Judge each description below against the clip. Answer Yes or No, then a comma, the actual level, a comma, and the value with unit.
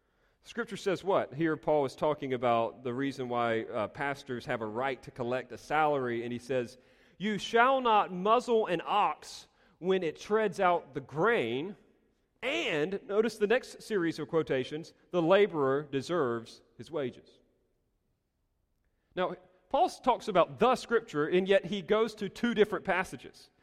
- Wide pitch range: Yes, wide, 7.9 semitones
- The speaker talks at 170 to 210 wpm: No, average, 155 wpm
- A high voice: No, medium, 160 Hz